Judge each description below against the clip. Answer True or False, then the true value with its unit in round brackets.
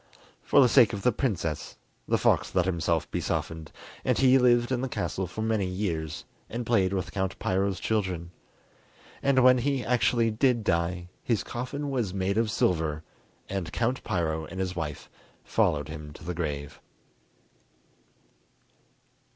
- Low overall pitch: True (95 Hz)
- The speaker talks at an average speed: True (155 wpm)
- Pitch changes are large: True (6.1 semitones)